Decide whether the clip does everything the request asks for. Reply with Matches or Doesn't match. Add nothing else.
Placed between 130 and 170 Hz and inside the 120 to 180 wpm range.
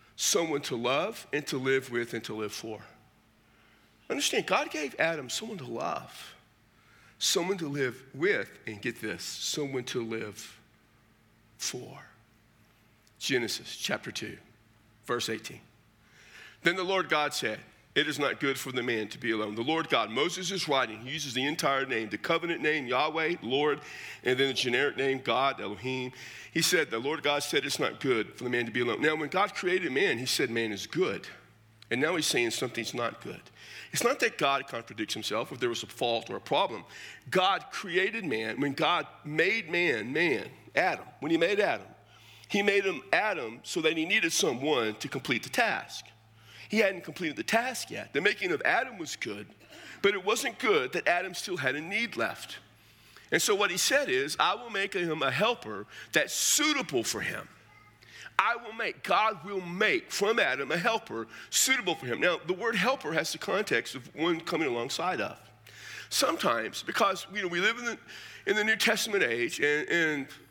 Doesn't match